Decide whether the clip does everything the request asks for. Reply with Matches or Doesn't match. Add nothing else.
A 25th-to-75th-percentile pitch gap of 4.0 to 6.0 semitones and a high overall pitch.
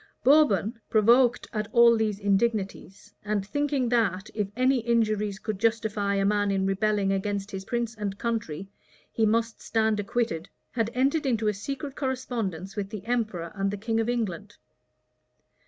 Doesn't match